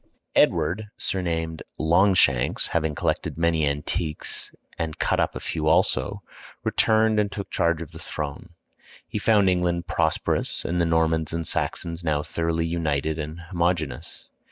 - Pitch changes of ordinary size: No, narrow, 2.0 semitones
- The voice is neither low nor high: No, very low, 85 Hz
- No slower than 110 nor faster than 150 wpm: Yes, average, 140 wpm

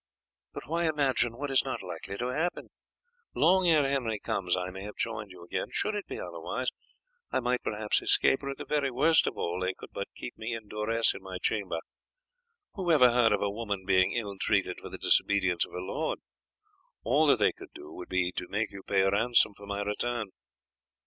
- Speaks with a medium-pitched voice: No, low, 110 Hz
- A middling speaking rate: No, fast, 210 wpm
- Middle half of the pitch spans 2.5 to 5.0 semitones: No, wide, 5.5 semitones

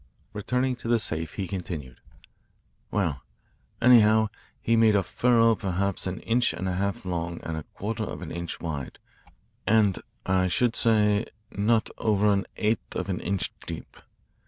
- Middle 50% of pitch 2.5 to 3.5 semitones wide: No, average, 3.9 semitones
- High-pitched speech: No, low, 100 Hz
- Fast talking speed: No, average, 155 wpm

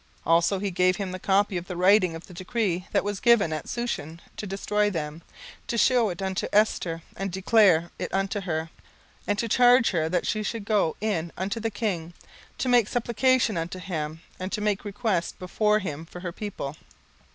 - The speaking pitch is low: No, high, 195 Hz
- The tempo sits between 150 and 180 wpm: No, average, 200 wpm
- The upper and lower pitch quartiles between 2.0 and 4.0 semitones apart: Yes, average, 3.7 semitones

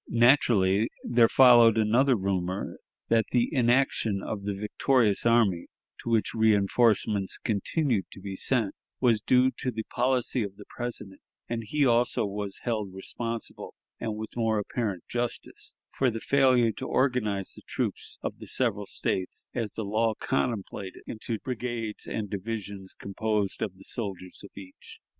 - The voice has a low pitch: Yes, low, 110 Hz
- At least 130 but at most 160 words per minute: Yes, average, 150 wpm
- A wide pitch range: No, average, 3.3 semitones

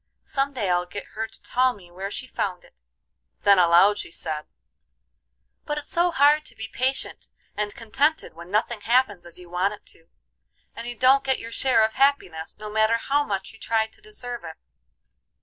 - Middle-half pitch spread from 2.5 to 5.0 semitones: No, wide, 5.5 semitones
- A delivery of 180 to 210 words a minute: Yes, average, 195 wpm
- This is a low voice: No, high, 220 Hz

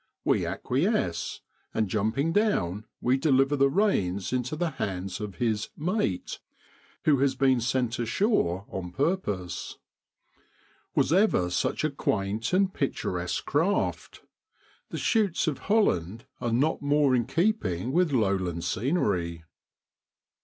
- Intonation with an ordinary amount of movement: No, wide, 8.4 semitones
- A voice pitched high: No, low, 130 Hz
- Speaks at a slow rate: Yes, slow, 125 wpm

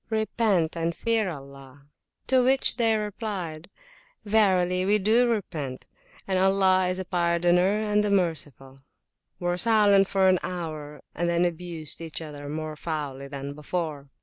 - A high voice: No, medium, 175 Hz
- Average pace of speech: No, slow, 130 wpm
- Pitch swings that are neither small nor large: Yes, average, 4.6 semitones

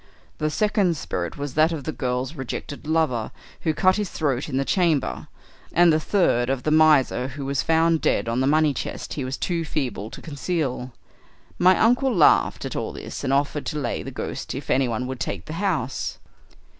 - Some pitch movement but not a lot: Yes, average, 3.9 semitones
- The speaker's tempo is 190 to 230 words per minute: Yes, average, 195 wpm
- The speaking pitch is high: No, medium, 150 Hz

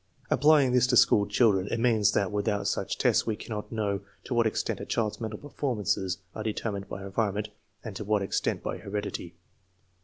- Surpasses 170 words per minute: Yes, average, 185 wpm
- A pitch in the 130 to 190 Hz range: No, low, 105 Hz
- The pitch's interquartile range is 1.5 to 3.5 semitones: Yes, narrow, 2.4 semitones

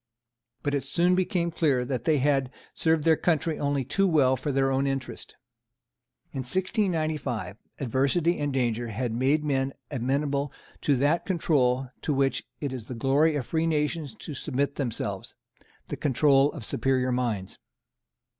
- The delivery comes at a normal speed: Yes, average, 155 wpm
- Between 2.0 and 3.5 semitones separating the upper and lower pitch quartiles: Yes, average, 3.2 semitones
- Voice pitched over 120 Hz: Yes, medium, 140 Hz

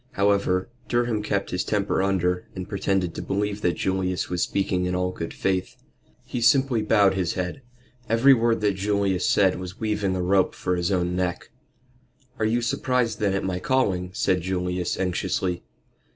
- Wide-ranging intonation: No, narrow, 2.6 semitones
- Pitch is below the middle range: Yes, very low, 95 Hz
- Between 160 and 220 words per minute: Yes, average, 170 wpm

